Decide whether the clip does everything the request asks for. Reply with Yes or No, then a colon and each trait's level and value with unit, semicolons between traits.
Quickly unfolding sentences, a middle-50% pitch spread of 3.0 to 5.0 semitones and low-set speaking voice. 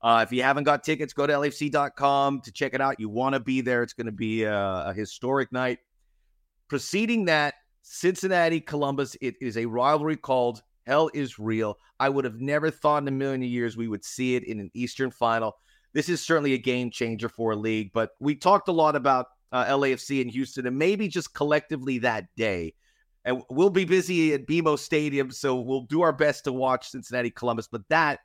Yes: fast, 210 wpm; average, 3.8 semitones; low, 130 Hz